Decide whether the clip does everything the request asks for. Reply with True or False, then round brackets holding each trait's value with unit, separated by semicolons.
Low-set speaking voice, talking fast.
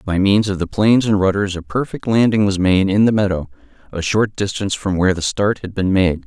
True (100 Hz; 240 wpm)